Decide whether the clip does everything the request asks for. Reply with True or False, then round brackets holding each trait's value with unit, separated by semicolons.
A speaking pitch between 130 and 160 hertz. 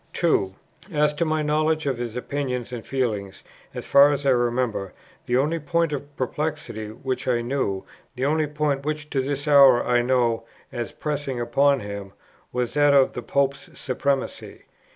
True (135 Hz)